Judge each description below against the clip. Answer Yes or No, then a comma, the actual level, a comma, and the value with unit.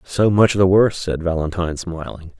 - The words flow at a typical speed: Yes, average, 175 wpm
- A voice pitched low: Yes, very low, 90 Hz